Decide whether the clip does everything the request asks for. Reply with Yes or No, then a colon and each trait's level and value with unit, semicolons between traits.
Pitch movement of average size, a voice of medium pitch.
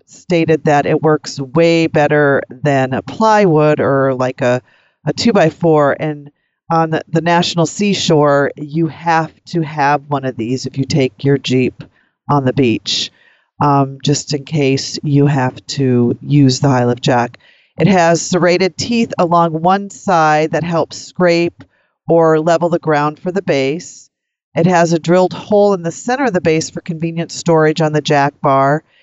Yes: average, 3.5 semitones; medium, 155 Hz